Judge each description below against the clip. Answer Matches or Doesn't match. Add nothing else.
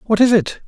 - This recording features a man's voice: Matches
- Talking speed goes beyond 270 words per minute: Doesn't match